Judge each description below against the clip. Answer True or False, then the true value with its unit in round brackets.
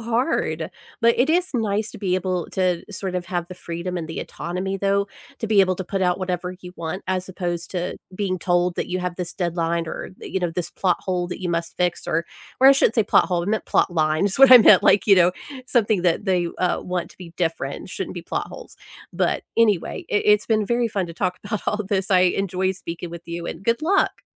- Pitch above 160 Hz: True (185 Hz)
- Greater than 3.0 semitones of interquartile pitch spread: False (2.7 semitones)